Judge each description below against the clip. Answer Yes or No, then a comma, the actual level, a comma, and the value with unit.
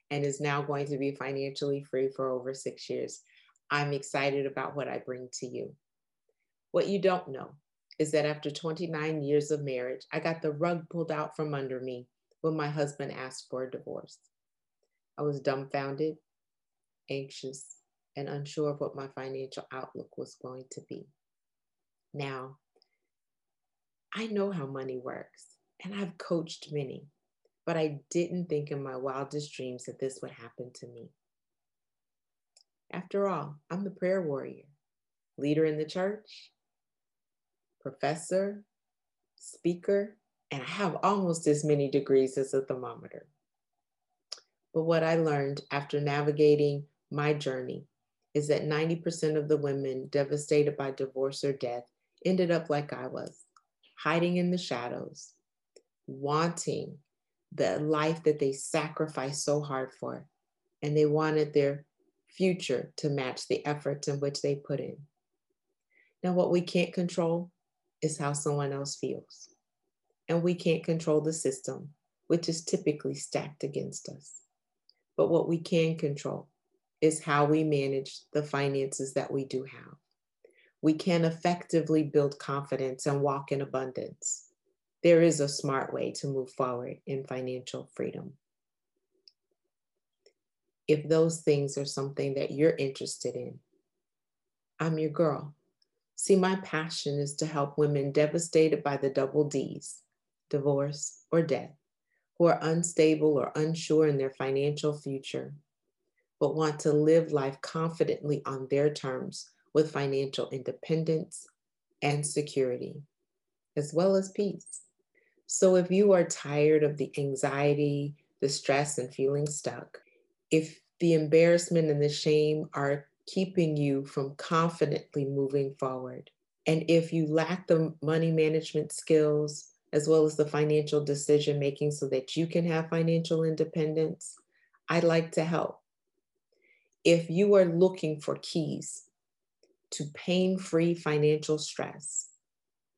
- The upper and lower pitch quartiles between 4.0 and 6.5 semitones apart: No, average, 3.3 semitones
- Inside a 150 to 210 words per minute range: No, average, 140 wpm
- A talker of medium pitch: Yes, medium, 150 Hz